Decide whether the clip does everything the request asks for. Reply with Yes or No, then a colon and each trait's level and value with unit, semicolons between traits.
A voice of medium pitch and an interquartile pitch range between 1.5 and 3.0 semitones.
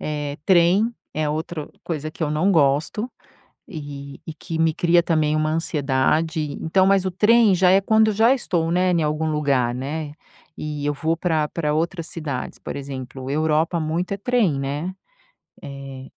No: medium, 155 Hz; average, 3.4 semitones